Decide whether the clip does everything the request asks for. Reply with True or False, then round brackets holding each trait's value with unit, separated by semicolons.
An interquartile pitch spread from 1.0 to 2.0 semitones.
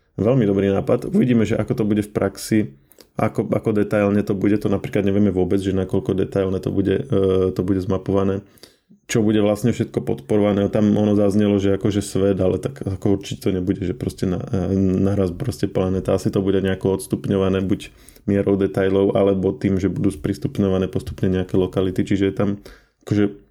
True (1.6 semitones)